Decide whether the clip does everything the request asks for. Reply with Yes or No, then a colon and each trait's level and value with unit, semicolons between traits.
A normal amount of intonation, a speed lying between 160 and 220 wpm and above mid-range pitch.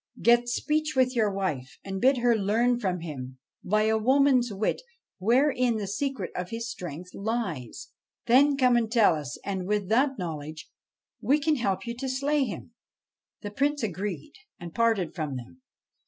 No: wide, 5.7 semitones; average, 170 wpm; high, 220 Hz